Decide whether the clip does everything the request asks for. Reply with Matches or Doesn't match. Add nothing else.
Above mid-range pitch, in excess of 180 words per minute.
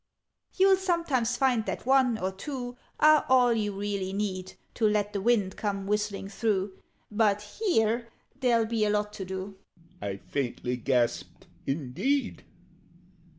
Doesn't match